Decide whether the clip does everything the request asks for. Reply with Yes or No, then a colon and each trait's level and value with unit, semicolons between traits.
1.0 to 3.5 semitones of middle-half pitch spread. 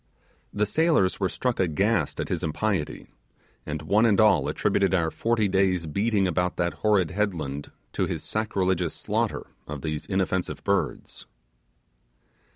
No: average, 4.2 semitones